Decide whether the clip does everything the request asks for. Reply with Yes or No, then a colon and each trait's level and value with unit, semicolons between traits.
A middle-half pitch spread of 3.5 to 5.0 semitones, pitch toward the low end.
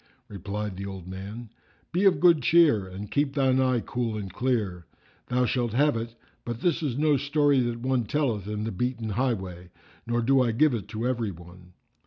Yes: average, 4.5 semitones; low, 120 Hz